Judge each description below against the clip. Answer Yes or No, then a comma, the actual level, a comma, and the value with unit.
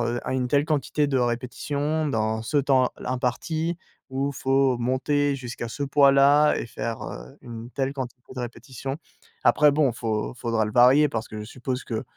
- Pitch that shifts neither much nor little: Yes, average, 3.1 semitones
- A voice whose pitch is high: No, low, 130 Hz